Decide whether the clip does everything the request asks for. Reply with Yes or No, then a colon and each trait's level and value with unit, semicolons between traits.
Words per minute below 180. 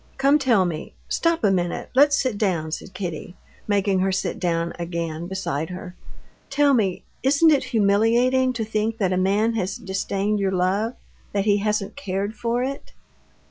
Yes: average, 170 wpm